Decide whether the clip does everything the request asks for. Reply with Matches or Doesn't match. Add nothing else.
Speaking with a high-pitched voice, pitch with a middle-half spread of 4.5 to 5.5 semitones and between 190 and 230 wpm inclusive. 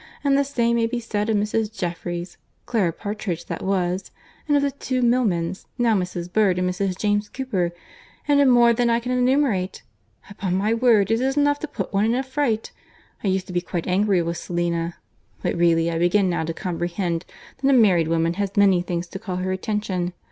Matches